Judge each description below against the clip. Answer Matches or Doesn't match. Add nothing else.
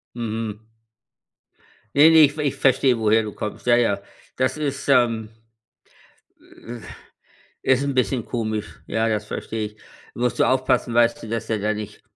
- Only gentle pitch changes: Doesn't match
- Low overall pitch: Matches